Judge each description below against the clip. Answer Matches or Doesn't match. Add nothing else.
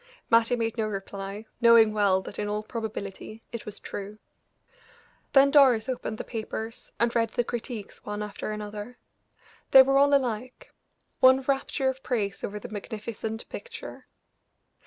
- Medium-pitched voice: Doesn't match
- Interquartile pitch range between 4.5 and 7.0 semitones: Doesn't match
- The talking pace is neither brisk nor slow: Matches